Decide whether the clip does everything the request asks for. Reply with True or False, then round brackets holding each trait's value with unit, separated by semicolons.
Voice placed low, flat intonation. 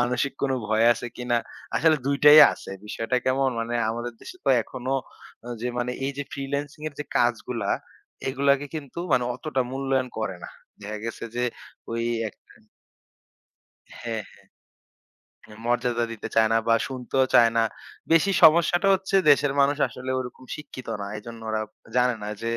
False (125 Hz; 3.1 semitones)